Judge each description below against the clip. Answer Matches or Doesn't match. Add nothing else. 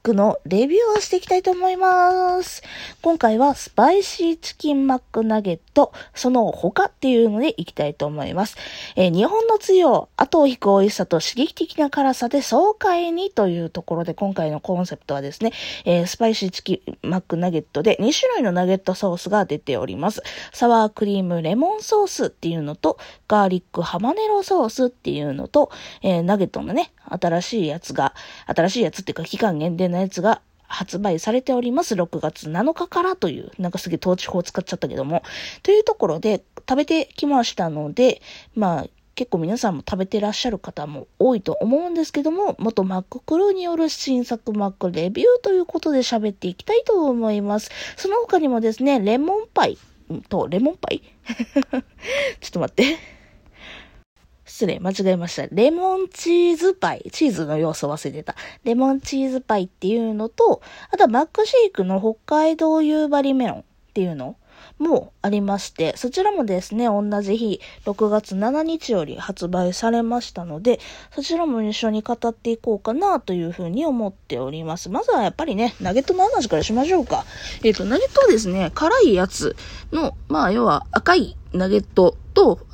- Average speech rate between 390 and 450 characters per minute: Doesn't match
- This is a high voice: Matches